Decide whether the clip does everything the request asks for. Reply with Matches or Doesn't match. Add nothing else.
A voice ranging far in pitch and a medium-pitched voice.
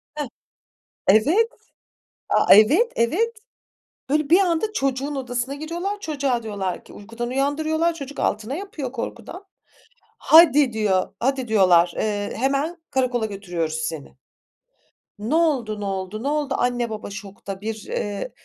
Doesn't match